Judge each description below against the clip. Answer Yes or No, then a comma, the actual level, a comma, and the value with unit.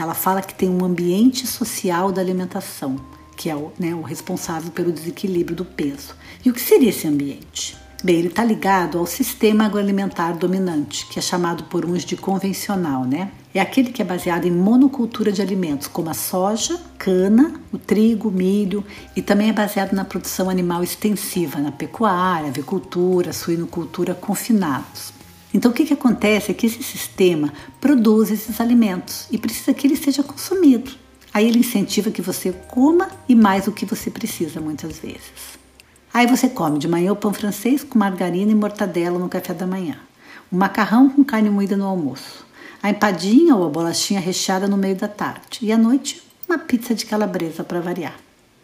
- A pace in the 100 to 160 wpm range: No, average, 180 wpm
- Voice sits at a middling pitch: No, high, 195 Hz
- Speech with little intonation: No, average, 4.1 semitones